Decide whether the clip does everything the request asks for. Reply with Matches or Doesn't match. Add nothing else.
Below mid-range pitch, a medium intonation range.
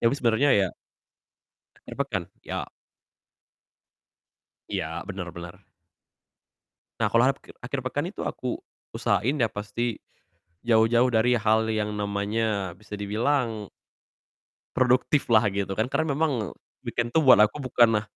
Matches